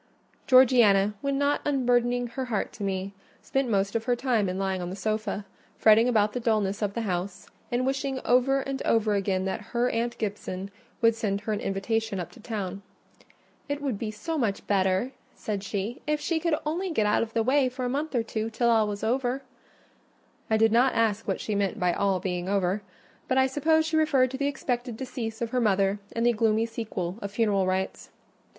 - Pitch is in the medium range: No, high, 225 Hz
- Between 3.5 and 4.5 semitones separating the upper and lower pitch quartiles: Yes, average, 4.1 semitones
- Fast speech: Yes, fast, 210 wpm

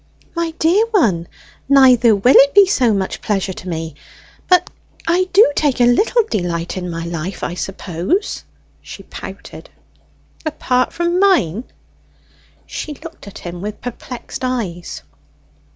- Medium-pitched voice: No, high, 245 Hz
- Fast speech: No, slow, 135 wpm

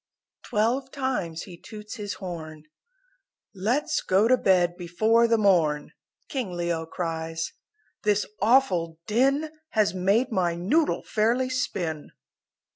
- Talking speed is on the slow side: Yes, slow, 120 wpm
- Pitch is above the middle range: Yes, high, 200 Hz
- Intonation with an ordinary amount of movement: No, wide, 5.7 semitones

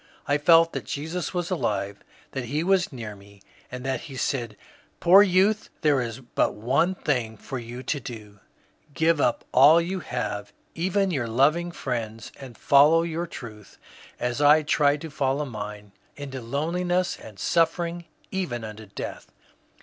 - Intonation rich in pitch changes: Yes, wide, 6.2 semitones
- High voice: No, medium, 140 Hz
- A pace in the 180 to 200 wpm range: No, average, 165 wpm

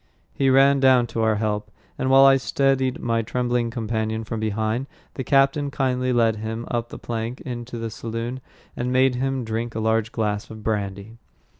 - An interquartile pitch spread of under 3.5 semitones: Yes, average, 2.7 semitones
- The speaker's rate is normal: Yes, average, 180 wpm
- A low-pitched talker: Yes, low, 120 Hz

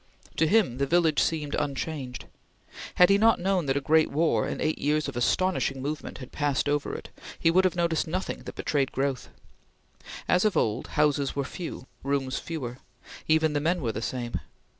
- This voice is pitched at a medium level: Yes, medium, 150 Hz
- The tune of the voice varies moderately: Yes, average, 3.7 semitones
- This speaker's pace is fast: No, average, 185 wpm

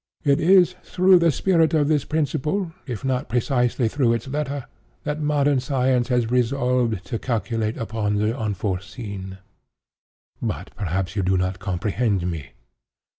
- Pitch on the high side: No, low, 125 Hz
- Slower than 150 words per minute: Yes, average, 140 wpm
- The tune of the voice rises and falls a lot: Yes, wide, 5.7 semitones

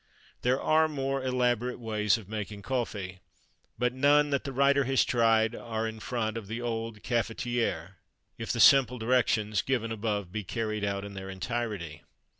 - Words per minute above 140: Yes, average, 165 wpm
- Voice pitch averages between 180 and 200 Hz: No, low, 115 Hz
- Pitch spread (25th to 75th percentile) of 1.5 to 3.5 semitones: Yes, average, 3.1 semitones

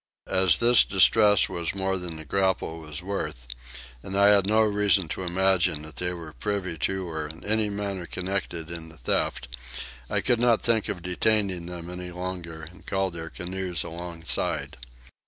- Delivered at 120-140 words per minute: No, average, 170 wpm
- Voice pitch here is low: Yes, very low, 90 Hz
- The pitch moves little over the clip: No, average, 3.0 semitones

